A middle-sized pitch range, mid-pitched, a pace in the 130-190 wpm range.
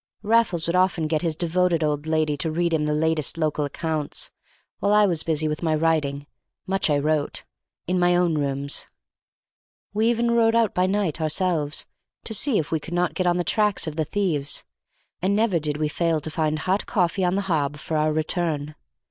No: average, 3.2 semitones; medium, 165 Hz; average, 200 wpm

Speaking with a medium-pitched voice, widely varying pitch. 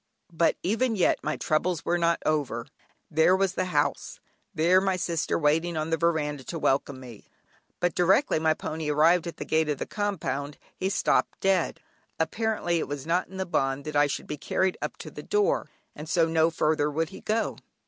No: medium, 165 Hz; average, 3.4 semitones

